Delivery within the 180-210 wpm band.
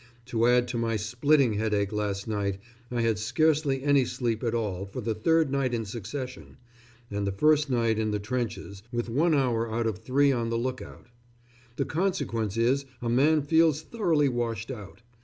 Yes: average, 185 wpm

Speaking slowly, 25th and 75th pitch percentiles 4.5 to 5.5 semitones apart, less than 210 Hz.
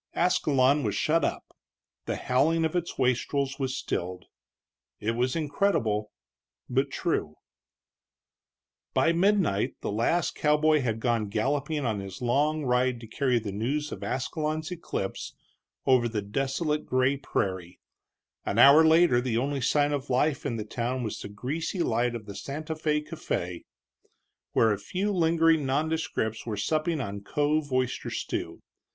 No: average, 145 wpm; average, 5.2 semitones; low, 135 Hz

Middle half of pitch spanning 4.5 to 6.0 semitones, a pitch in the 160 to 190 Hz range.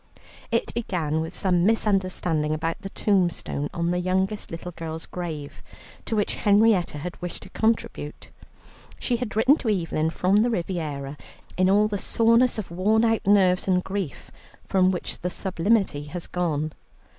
No: average, 4.0 semitones; medium, 185 Hz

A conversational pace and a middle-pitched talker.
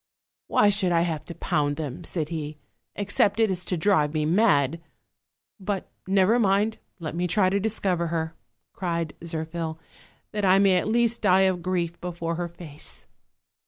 Yes: average, 170 wpm; medium, 175 Hz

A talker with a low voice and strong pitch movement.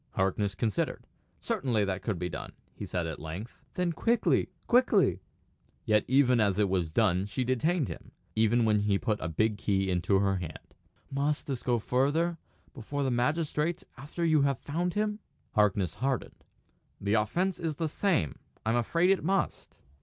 Yes: low, 120 Hz; wide, 7.6 semitones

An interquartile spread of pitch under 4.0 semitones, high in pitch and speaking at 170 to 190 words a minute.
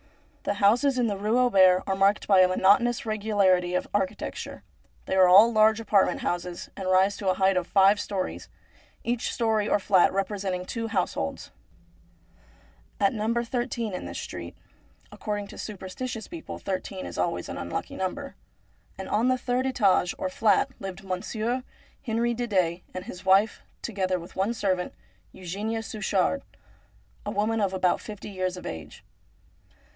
No: average, 3.3 semitones; high, 200 Hz; average, 160 wpm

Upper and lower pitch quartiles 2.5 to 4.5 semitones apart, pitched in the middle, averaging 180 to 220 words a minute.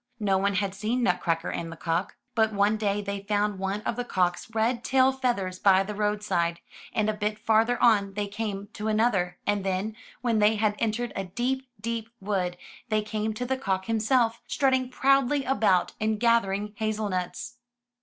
No: average, 2.9 semitones; high, 210 Hz; average, 185 wpm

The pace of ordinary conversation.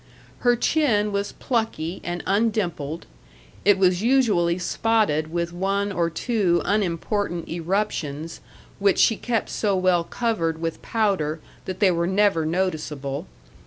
No: slow, 125 wpm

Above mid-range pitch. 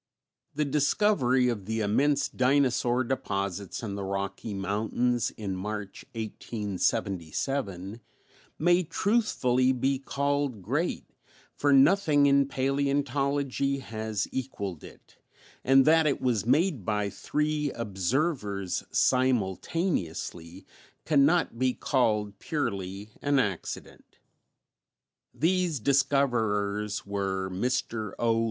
No: low, 125 Hz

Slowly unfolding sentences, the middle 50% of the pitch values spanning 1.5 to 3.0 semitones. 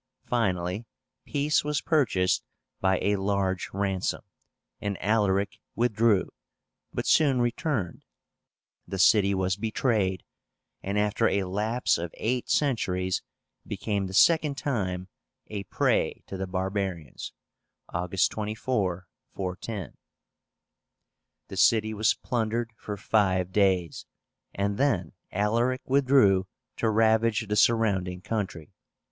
No: slow, 110 wpm; average, 3.4 semitones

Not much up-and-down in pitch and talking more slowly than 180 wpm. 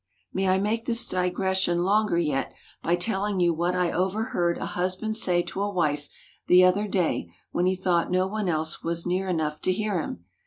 No: narrow, 2.2 semitones; average, 195 wpm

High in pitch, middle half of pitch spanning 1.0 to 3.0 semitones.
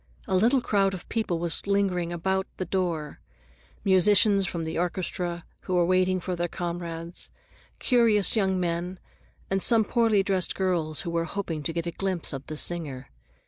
No: medium, 180 Hz; narrow, 2.5 semitones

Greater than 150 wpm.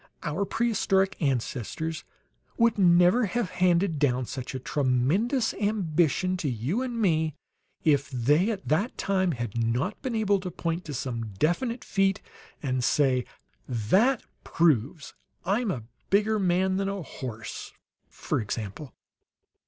No: slow, 135 wpm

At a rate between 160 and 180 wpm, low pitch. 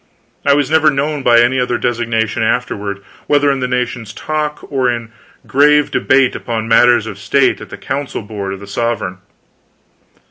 Yes: average, 170 wpm; low, 120 Hz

